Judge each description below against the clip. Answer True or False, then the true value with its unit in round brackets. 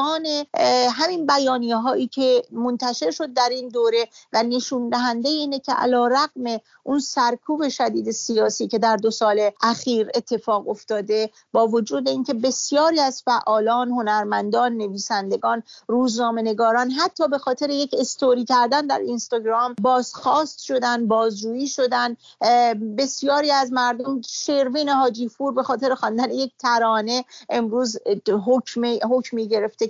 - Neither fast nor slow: False (125 wpm)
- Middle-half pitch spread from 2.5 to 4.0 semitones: True (2.8 semitones)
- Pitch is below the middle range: False (245 Hz)